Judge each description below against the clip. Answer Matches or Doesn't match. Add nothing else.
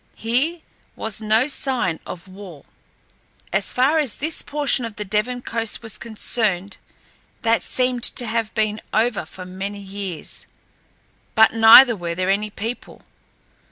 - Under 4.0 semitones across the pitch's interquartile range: Matches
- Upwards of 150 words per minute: Doesn't match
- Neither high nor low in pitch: Doesn't match